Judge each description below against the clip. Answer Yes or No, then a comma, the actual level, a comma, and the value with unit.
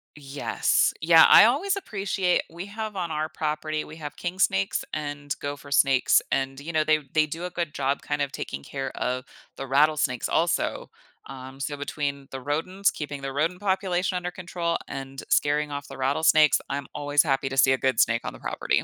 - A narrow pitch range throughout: No, average, 3.8 semitones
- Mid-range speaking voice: Yes, medium, 150 Hz